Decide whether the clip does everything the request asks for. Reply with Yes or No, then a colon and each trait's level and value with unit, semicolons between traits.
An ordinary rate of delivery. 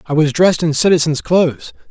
Yes: average, 190 wpm